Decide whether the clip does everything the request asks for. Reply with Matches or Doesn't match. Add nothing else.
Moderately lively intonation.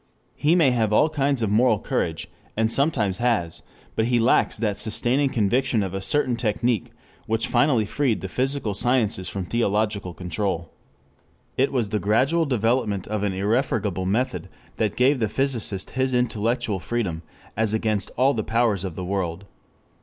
Matches